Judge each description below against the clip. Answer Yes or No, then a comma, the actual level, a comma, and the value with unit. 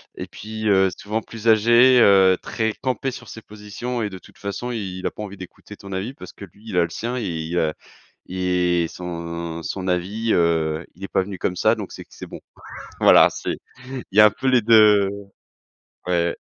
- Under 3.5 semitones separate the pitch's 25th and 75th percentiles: No, average, 3.9 semitones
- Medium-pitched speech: No, low, 100 Hz